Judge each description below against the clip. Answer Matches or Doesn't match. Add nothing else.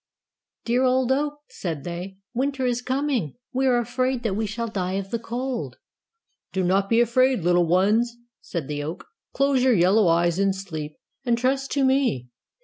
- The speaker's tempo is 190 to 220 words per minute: Doesn't match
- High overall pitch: Matches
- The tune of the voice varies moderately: Doesn't match